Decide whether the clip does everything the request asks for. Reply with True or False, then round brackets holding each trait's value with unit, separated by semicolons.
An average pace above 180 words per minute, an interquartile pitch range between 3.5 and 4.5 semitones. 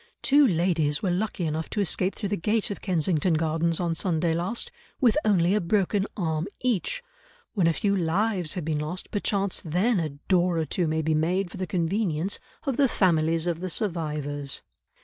True (190 wpm; 3.8 semitones)